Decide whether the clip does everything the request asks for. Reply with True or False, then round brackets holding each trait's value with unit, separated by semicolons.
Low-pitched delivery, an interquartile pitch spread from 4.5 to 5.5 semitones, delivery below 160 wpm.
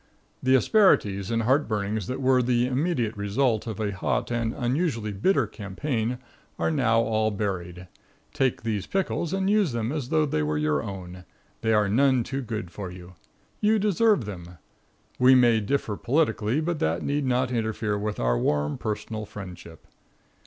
False (115 Hz; 4.8 semitones; 165 wpm)